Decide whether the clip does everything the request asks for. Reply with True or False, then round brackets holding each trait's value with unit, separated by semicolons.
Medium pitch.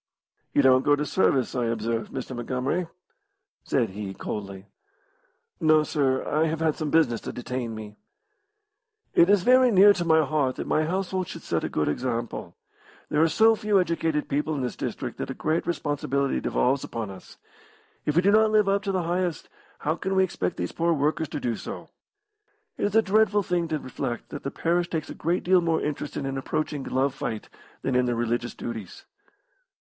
True (150 Hz)